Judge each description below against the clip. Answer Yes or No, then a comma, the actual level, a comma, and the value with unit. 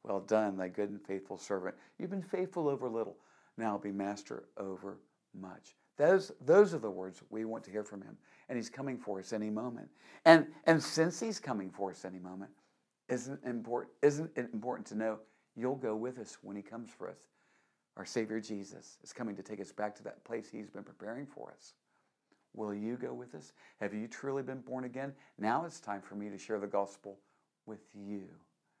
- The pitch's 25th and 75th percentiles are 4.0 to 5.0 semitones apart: Yes, average, 4.4 semitones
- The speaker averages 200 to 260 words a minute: Yes, fast, 205 wpm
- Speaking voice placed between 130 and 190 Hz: No, low, 110 Hz